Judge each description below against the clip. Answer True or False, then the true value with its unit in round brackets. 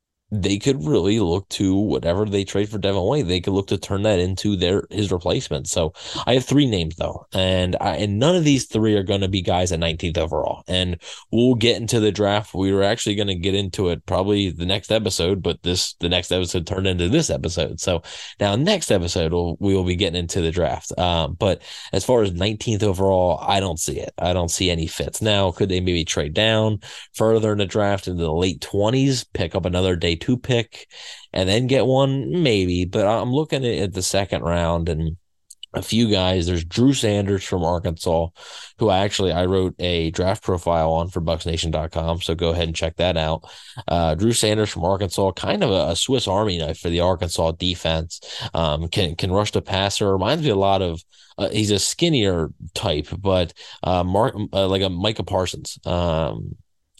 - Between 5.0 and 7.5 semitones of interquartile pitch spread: False (3.4 semitones)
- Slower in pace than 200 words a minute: False (205 wpm)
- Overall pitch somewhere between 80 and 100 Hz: True (95 Hz)